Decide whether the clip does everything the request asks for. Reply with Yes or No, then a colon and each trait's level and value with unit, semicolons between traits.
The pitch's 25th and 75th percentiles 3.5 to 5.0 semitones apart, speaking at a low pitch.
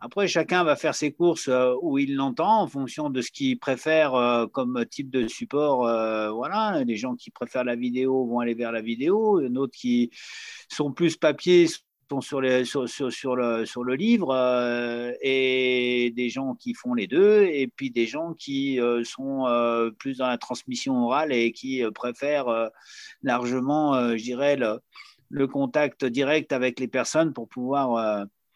Yes: average, 4.2 semitones; low, 130 Hz